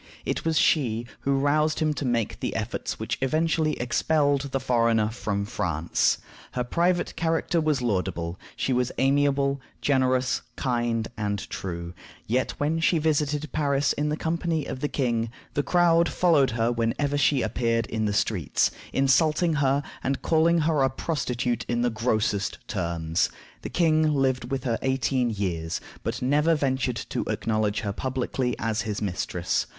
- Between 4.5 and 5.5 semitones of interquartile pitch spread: Yes, average, 4.8 semitones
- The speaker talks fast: No, average, 155 wpm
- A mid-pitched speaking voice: No, low, 130 Hz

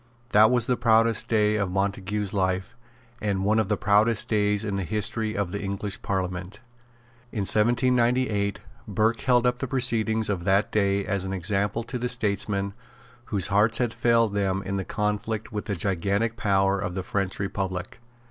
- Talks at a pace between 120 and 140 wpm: No, average, 175 wpm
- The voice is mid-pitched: No, low, 105 Hz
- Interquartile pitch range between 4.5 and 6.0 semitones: No, narrow, 2.4 semitones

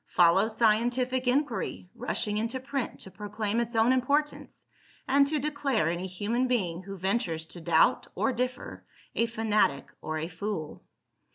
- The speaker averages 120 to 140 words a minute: No, average, 150 wpm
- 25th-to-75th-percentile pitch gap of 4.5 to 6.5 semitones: Yes, average, 5.0 semitones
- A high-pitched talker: Yes, high, 225 Hz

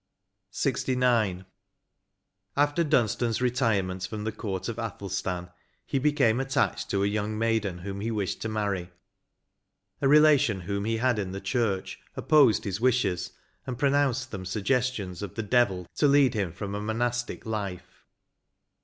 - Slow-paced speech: No, average, 155 wpm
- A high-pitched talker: No, low, 110 Hz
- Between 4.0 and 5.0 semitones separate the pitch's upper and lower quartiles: Yes, average, 4.3 semitones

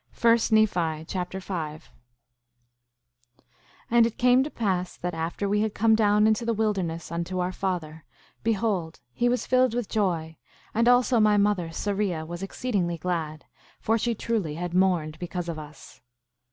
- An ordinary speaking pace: Yes, average, 160 wpm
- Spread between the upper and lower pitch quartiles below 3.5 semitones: No, average, 4.6 semitones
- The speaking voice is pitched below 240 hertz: Yes, high, 190 Hz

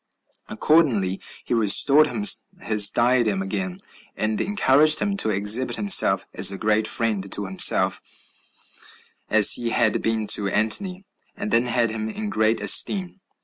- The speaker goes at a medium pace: Yes, average, 145 wpm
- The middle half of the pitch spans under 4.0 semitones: No, average, 5.0 semitones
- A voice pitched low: Yes, low, 110 Hz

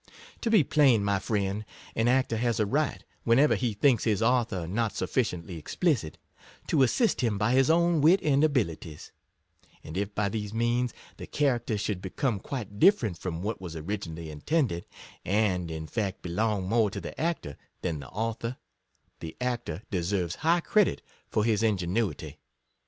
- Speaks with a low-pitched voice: Yes, low, 110 Hz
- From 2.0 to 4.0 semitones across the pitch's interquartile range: No, average, 5.3 semitones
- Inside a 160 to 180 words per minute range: Yes, average, 165 wpm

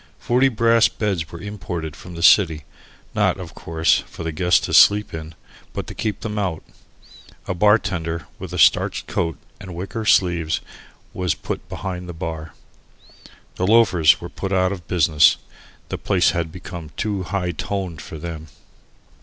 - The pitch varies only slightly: No, average, 3.3 semitones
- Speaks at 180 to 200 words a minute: No, average, 165 wpm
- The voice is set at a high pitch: No, very low, 90 Hz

